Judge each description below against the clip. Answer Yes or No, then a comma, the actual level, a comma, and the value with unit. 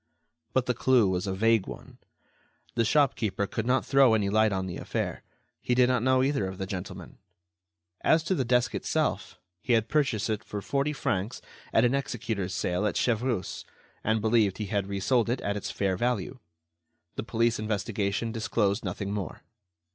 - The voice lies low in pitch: Yes, low, 110 Hz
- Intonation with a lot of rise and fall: No, average, 3.8 semitones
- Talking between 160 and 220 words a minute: Yes, average, 175 wpm